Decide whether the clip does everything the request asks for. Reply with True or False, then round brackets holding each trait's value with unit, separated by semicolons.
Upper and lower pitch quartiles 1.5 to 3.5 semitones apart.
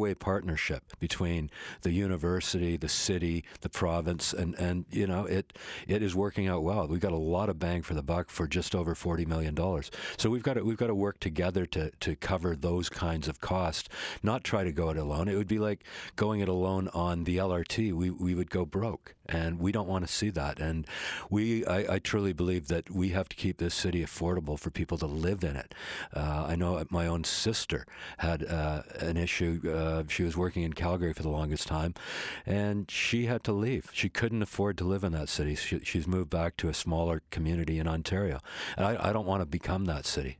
True (2.7 semitones)